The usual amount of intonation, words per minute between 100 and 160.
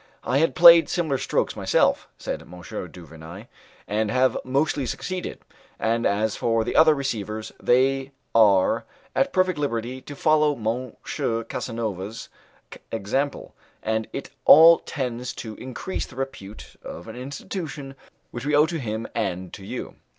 Yes: average, 4.6 semitones; average, 145 wpm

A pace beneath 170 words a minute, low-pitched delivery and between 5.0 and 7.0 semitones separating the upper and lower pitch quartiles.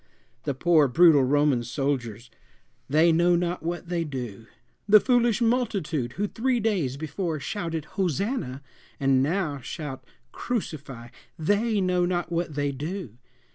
No: slow, 135 wpm; medium, 160 Hz; wide, 5.5 semitones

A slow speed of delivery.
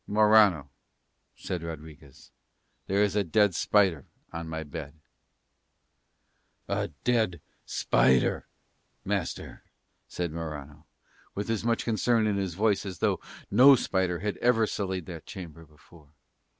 Yes: slow, 125 wpm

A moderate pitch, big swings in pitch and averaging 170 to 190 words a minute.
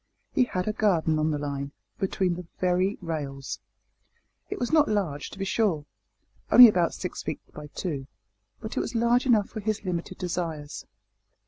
Yes: medium, 180 Hz; wide, 5.7 semitones; average, 175 wpm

